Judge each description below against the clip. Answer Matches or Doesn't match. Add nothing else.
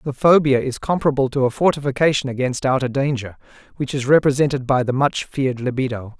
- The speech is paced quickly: Doesn't match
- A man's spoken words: Matches